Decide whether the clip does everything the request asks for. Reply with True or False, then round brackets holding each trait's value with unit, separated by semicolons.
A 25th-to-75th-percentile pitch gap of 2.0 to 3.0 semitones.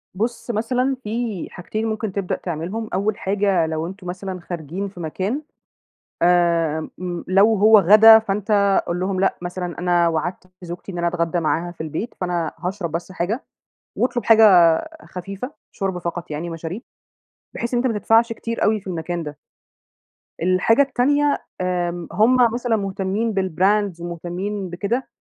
False (3.8 semitones)